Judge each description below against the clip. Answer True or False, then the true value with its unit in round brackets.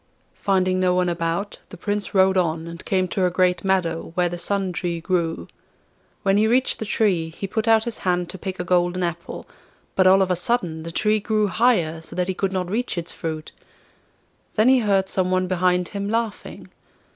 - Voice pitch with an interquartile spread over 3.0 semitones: False (2.5 semitones)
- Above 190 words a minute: True (205 wpm)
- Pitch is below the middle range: False (185 Hz)